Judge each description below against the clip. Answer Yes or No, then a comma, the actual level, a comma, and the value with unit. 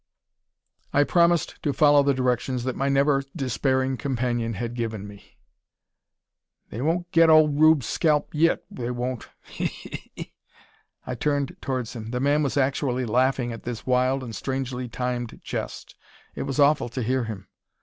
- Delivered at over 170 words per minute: No, average, 160 wpm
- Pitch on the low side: Yes, low, 130 Hz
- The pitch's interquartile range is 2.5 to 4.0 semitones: Yes, average, 2.8 semitones